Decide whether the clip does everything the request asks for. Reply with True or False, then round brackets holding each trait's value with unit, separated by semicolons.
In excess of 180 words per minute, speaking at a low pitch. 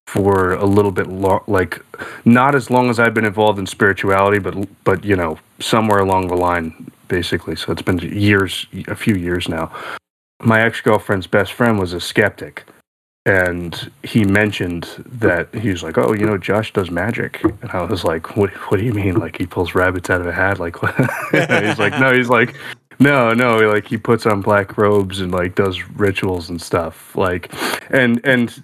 True (195 wpm; 100 Hz)